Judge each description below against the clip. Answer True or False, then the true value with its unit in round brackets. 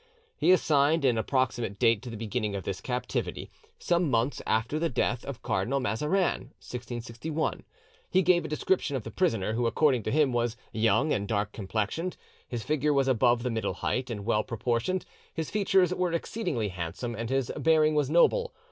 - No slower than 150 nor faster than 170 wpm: False (180 wpm)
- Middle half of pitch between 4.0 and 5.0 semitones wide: False (5.5 semitones)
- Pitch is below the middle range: True (125 Hz)